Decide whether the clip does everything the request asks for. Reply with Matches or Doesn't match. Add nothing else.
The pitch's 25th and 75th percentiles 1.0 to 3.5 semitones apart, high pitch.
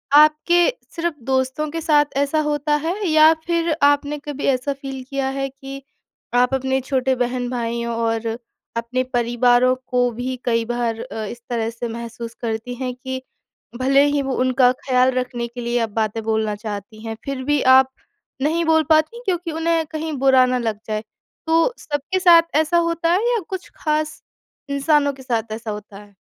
Doesn't match